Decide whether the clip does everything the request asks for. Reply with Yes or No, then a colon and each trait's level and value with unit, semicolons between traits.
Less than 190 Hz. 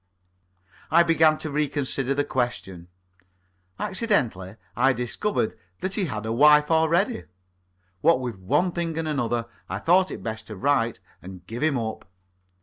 Yes: medium, 140 Hz